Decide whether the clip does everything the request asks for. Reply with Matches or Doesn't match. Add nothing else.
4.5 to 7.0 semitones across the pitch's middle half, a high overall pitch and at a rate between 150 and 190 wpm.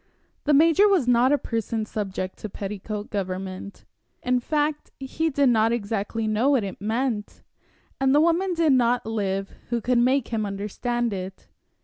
Matches